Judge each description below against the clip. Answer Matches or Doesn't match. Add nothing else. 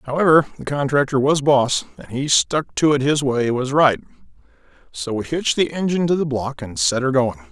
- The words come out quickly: Matches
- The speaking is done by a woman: Doesn't match